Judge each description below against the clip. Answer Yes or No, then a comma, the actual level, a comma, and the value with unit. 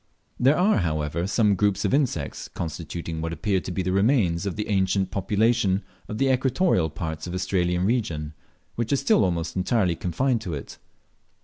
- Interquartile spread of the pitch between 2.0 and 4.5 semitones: No, average, 5.1 semitones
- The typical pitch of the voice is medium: No, very low, 95 Hz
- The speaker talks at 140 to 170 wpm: No, average, 180 wpm